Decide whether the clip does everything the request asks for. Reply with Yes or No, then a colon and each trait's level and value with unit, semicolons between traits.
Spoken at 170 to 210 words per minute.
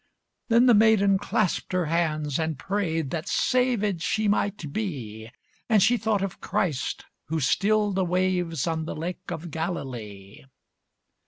No: average, 145 wpm